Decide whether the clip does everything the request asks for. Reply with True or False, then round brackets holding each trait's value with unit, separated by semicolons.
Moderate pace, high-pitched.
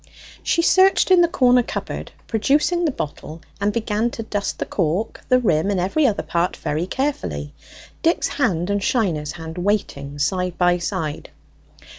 True (160 wpm; 200 Hz)